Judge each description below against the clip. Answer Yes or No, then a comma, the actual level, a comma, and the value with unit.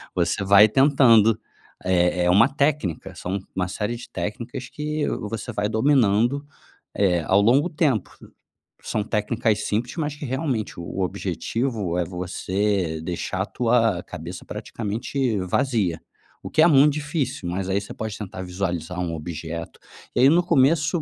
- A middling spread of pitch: No, wide, 6.0 semitones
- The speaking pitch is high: No, low, 110 Hz